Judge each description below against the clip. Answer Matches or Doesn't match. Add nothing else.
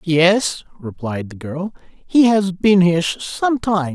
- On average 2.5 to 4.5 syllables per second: Matches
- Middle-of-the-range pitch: Matches